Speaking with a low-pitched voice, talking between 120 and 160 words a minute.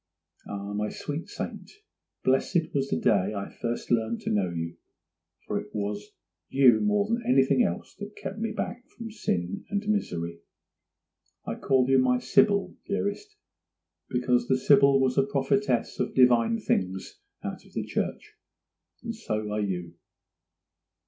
Yes: low, 130 Hz; average, 150 wpm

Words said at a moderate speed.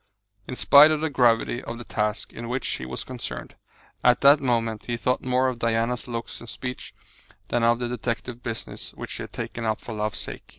No: fast, 210 wpm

